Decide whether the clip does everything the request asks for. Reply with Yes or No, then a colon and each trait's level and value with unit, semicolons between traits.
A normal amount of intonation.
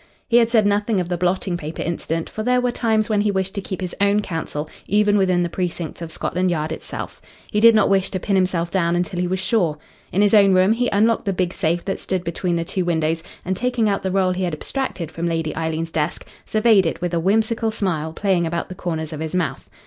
Yes: average, 3.5 semitones